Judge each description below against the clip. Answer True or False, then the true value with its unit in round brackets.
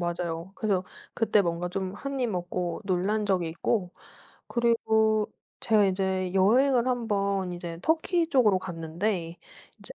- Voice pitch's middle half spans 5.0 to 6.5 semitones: False (3.9 semitones)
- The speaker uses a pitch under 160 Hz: False (195 Hz)